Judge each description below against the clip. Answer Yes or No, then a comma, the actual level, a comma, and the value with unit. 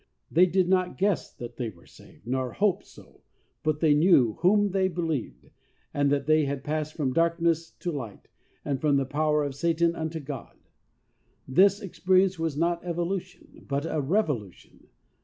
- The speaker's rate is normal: Yes, average, 165 wpm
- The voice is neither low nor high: Yes, medium, 160 Hz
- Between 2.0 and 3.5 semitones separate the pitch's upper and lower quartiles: No, average, 4.1 semitones